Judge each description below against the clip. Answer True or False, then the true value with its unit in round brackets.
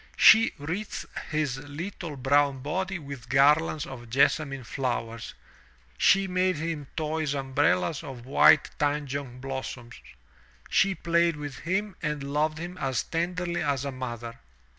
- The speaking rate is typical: False (130 wpm)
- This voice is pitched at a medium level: True (145 Hz)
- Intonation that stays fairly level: False (3.9 semitones)